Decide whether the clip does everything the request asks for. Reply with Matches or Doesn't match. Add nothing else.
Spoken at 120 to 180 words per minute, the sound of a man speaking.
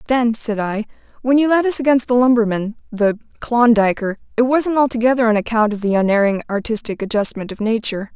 Doesn't match